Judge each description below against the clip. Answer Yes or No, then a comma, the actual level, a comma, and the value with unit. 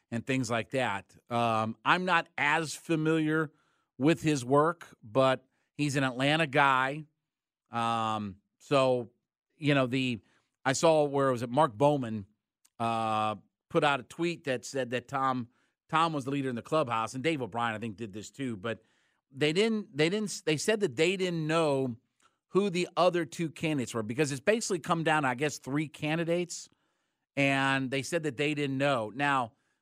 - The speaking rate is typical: Yes, average, 175 wpm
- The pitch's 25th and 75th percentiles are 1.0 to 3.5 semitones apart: No, average, 4.5 semitones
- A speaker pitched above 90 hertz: Yes, medium, 140 Hz